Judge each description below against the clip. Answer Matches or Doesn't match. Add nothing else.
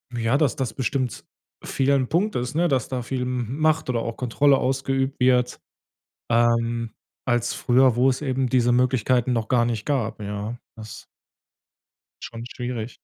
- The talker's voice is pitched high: Doesn't match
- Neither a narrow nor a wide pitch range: Doesn't match